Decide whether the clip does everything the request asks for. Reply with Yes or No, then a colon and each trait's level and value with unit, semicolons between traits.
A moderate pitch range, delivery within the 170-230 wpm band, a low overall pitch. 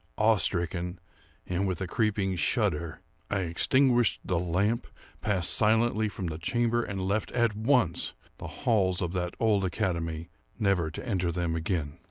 No: average, 4.1 semitones; average, 155 wpm; very low, 95 Hz